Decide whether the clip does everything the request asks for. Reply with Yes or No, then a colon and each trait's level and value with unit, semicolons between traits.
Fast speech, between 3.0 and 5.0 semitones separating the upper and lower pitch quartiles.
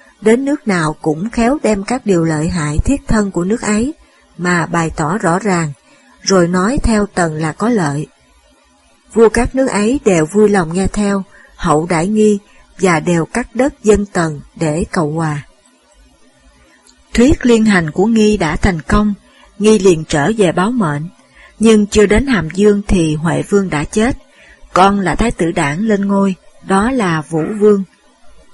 No: average, 175 wpm; average, 4.3 semitones